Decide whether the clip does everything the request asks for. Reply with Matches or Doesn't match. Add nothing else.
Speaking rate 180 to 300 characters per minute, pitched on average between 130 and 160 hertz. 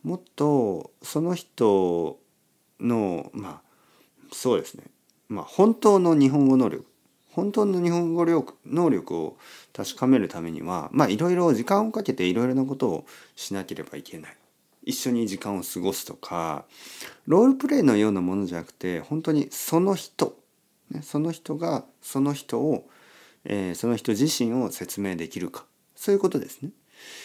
Matches